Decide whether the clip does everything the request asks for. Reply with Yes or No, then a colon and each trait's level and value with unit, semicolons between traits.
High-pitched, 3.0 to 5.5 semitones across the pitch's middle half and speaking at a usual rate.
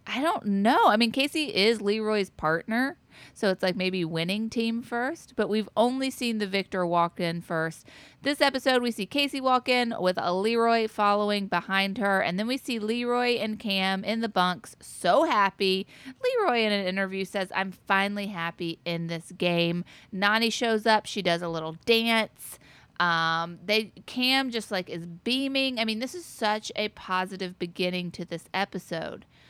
Yes: high, 205 Hz; average, 4.2 semitones; average, 175 wpm